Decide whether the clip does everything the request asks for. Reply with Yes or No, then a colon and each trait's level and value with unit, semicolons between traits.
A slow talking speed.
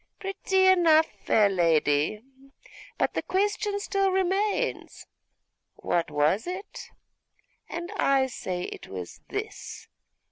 Yes: slow, 105 wpm